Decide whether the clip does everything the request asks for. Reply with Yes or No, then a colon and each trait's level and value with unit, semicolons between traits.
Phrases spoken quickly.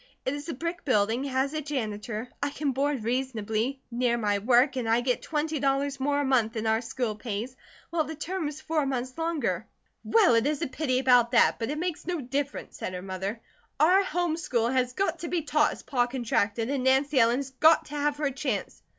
Yes: fast, 220 wpm